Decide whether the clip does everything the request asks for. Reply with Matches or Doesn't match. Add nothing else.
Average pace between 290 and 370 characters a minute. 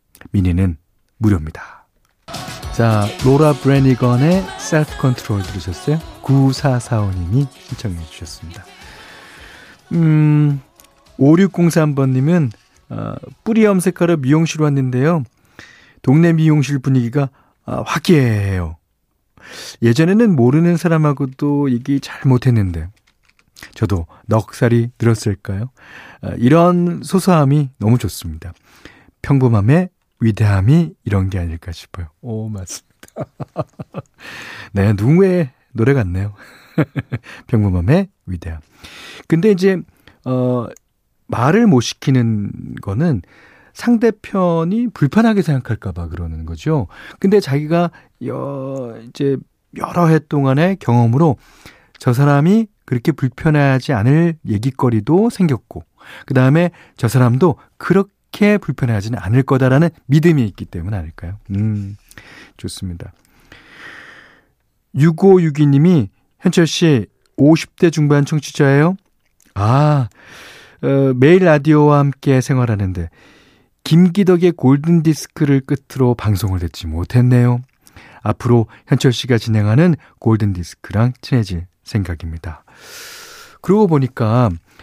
Doesn't match